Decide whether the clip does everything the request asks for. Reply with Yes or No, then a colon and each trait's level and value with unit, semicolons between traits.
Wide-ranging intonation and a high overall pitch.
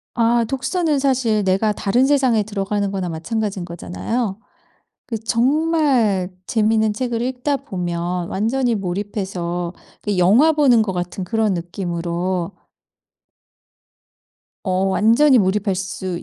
No: average, 4.7 semitones; high, 210 Hz